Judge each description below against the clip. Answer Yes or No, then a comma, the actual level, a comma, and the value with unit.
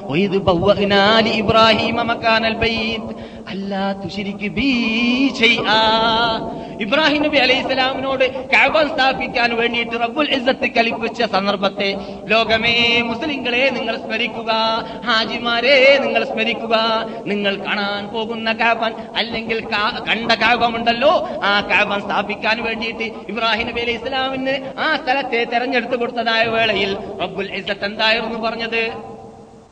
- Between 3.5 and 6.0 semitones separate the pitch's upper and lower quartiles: No, narrow, 2.5 semitones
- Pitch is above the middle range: Yes, high, 225 Hz